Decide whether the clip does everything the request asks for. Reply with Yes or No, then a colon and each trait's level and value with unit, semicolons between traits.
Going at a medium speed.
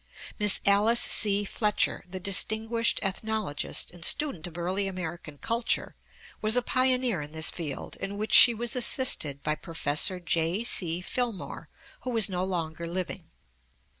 Yes: average, 145 wpm